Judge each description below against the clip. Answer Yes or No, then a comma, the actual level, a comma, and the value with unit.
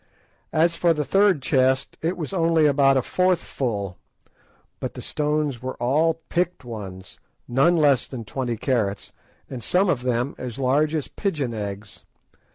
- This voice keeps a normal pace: Yes, average, 160 wpm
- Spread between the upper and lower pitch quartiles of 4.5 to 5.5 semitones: Yes, average, 5.1 semitones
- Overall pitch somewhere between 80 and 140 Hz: Yes, low, 135 Hz